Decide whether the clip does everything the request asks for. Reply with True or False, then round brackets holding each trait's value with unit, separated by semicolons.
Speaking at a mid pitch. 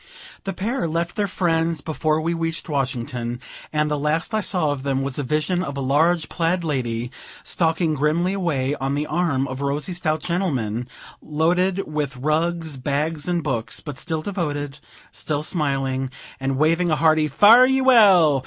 True (155 Hz)